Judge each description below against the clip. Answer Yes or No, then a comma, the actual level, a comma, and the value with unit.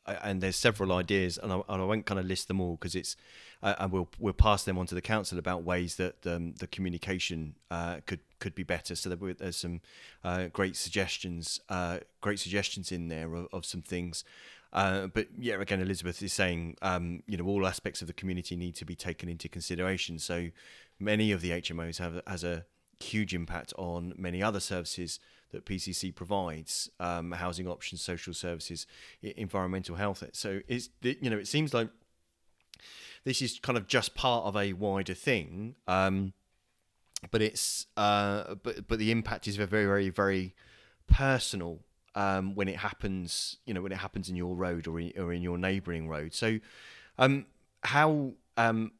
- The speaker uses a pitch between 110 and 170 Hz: No, very low, 95 Hz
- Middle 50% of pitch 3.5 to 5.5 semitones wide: No, narrow, 2.5 semitones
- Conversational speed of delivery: Yes, average, 185 wpm